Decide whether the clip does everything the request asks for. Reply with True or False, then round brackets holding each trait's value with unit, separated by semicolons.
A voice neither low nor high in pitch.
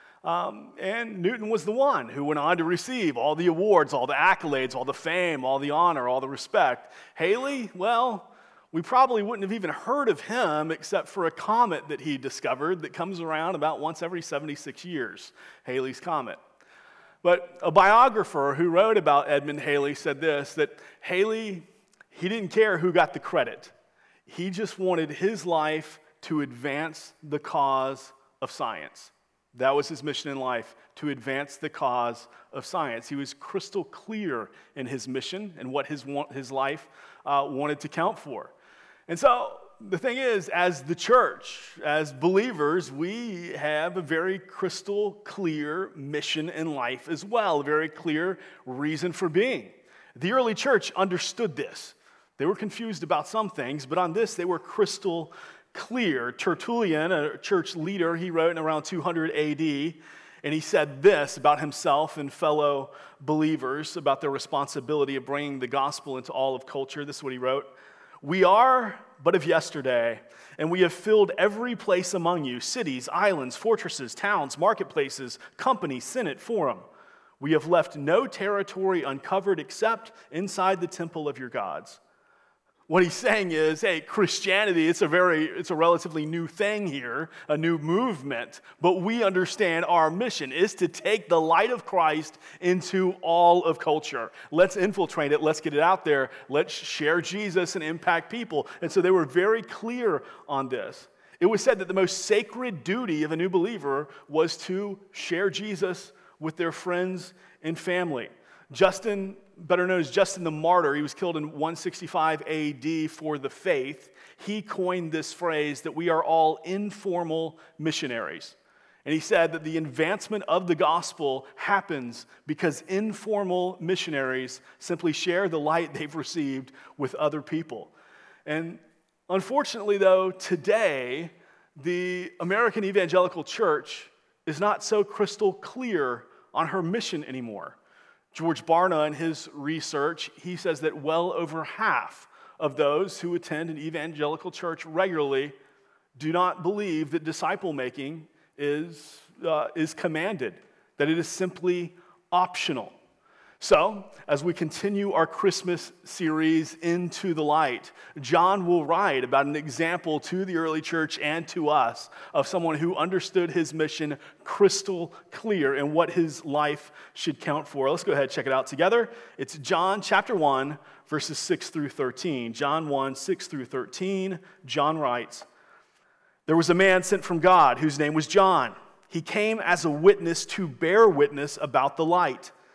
True (170 Hz)